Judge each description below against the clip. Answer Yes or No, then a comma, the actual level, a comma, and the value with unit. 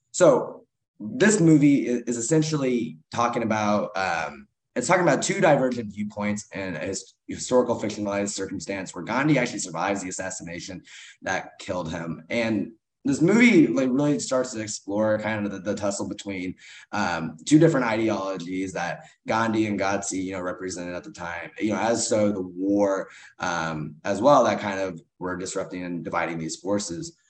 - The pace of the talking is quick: No, average, 165 wpm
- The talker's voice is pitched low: Yes, low, 105 Hz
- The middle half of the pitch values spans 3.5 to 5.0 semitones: Yes, average, 4.1 semitones